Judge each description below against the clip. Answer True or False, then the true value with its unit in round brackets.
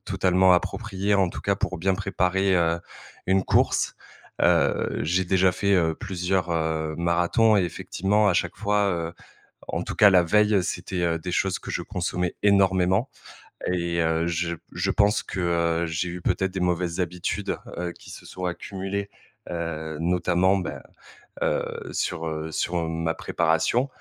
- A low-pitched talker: True (90 Hz)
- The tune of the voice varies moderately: False (2.2 semitones)